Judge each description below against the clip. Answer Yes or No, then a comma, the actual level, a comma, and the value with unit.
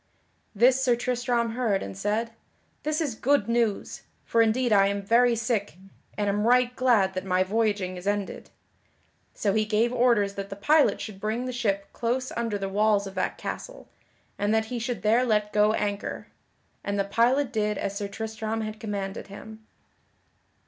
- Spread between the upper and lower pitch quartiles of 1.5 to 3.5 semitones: Yes, average, 2.9 semitones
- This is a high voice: Yes, high, 220 Hz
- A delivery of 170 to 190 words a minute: Yes, average, 175 wpm